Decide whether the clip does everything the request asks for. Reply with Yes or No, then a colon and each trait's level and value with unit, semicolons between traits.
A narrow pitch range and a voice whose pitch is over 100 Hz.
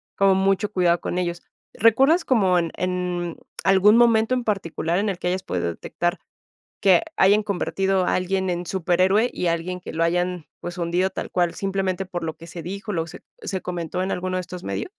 Yes: narrow, 2.0 semitones; medium, 185 Hz